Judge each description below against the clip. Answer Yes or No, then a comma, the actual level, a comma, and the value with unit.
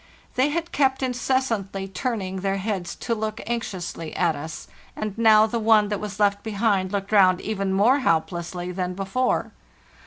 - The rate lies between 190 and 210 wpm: No, average, 160 wpm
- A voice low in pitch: No, high, 205 Hz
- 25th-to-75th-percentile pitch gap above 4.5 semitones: No, average, 3.3 semitones